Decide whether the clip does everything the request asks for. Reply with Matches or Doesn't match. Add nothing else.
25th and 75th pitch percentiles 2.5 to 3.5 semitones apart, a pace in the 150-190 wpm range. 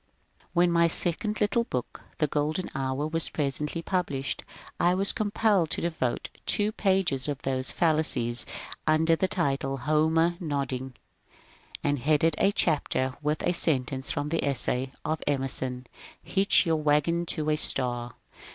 Doesn't match